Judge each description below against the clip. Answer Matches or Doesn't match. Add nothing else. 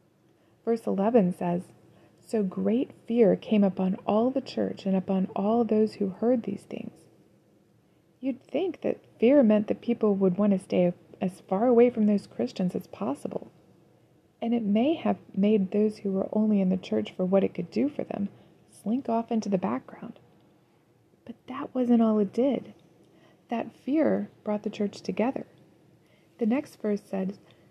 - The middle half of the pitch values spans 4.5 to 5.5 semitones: Doesn't match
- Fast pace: Doesn't match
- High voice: Matches